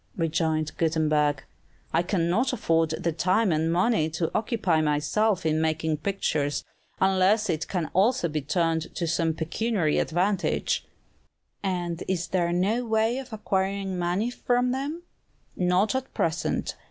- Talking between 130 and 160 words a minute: Yes, slow, 135 wpm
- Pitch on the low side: No, medium, 175 Hz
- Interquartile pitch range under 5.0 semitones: Yes, average, 4.6 semitones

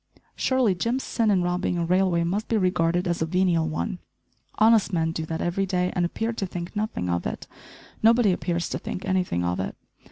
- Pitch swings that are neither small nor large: Yes, average, 3.3 semitones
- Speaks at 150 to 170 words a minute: No, average, 200 wpm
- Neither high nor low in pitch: Yes, medium, 180 Hz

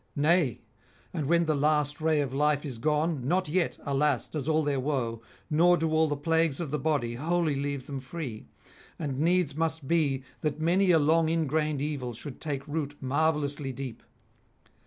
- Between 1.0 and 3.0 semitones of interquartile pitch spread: Yes, narrow, 2.6 semitones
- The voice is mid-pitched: Yes, medium, 150 Hz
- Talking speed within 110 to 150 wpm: No, average, 180 wpm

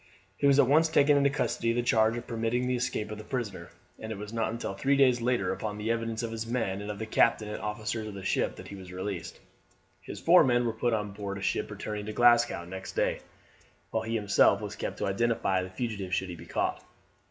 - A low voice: Yes, low, 110 Hz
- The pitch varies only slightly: No, average, 3.1 semitones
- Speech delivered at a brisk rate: Yes, fast, 245 wpm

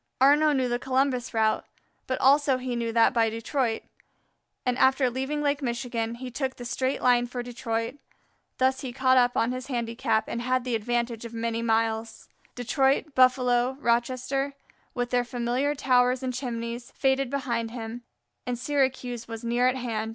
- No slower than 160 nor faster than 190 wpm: Yes, average, 165 wpm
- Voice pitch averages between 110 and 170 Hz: No, high, 245 Hz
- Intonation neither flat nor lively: No, narrow, 1.9 semitones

